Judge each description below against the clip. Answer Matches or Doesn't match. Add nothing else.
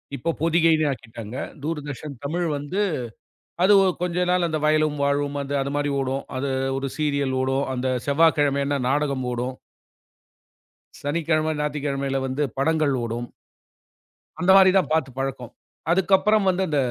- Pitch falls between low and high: Matches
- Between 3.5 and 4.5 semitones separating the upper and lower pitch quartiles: Doesn't match